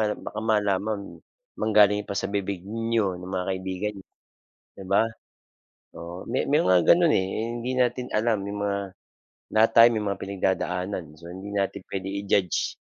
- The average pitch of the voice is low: Yes, low, 100 Hz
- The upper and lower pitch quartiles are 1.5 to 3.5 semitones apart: Yes, narrow, 2.6 semitones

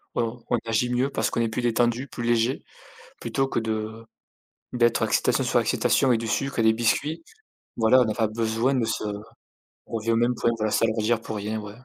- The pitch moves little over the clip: Yes, narrow, 1.6 semitones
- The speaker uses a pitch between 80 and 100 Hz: No, low, 115 Hz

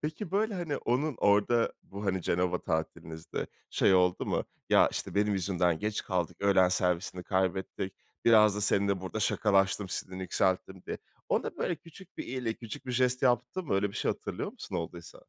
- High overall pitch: No, low, 100 Hz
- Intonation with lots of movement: No, average, 4.9 semitones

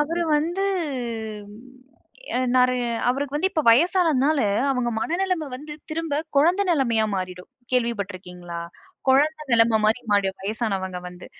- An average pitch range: No, wide, 7.1 semitones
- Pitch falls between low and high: No, very high, 255 Hz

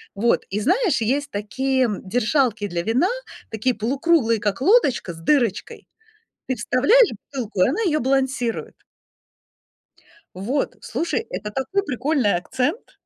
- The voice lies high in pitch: Yes, very high, 255 Hz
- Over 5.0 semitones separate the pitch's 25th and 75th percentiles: Yes, wide, 5.5 semitones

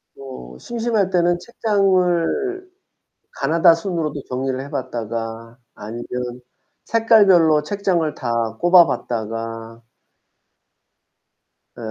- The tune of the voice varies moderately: No, wide, 8.1 semitones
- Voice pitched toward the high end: No, medium, 155 Hz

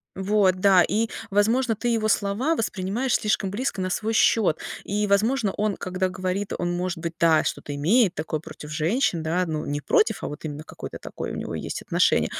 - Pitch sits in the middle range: No, high, 195 Hz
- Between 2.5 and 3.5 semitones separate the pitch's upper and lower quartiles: No, average, 4.1 semitones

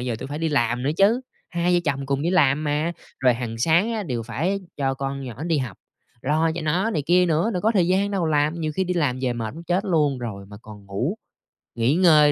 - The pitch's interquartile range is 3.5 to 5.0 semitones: No, wide, 5.4 semitones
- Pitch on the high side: No, medium, 150 Hz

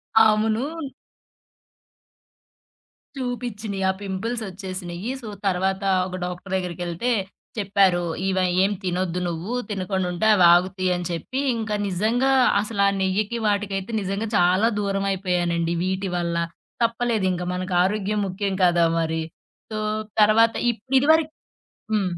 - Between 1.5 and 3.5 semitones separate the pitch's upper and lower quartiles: Yes, average, 3.2 semitones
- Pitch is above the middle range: Yes, high, 195 Hz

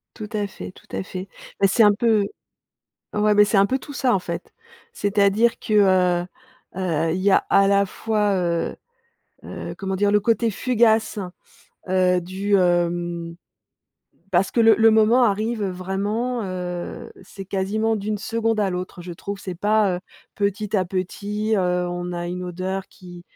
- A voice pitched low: No, high, 195 Hz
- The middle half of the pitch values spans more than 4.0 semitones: No, average, 2.9 semitones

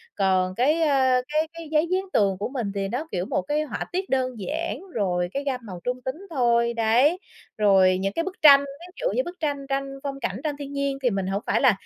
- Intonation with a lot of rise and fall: Yes, wide, 6.6 semitones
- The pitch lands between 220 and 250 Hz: No, very high, 265 Hz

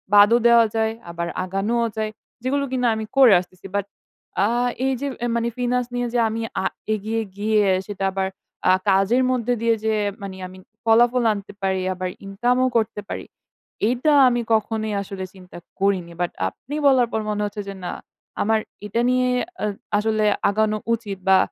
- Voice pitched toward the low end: No, high, 220 Hz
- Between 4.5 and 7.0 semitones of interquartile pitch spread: No, average, 3.4 semitones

